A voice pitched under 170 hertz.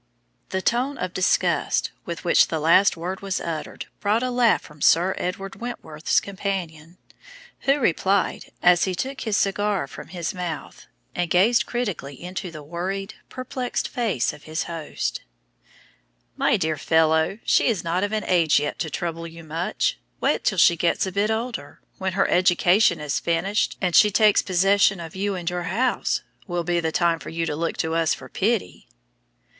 No: medium, 180 Hz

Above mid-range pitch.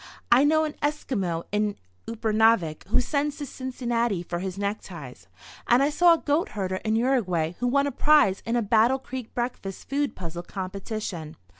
Yes: high, 225 Hz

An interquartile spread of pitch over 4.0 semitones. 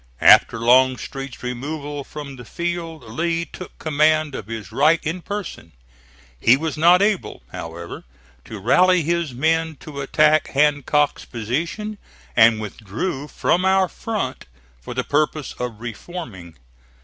Yes: wide, 5.5 semitones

